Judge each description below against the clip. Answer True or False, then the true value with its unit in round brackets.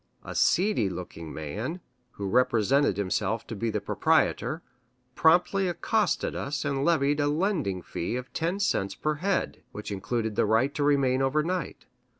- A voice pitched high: False (135 Hz)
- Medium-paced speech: True (155 wpm)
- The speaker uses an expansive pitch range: True (7.2 semitones)